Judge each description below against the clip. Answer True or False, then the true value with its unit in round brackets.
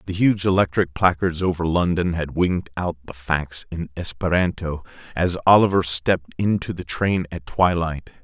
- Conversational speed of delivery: True (155 wpm)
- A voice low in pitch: True (85 Hz)